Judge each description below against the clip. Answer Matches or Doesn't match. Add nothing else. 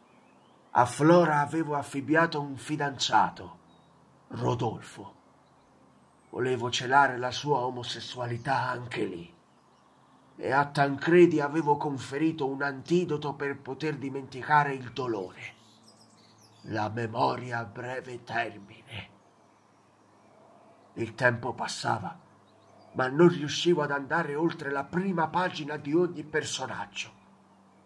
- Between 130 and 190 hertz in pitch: Matches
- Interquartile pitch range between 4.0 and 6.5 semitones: Doesn't match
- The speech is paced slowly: Matches